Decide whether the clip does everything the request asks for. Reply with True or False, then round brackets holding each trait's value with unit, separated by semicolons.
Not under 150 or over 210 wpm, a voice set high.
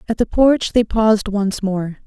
True (205 wpm; 210 Hz)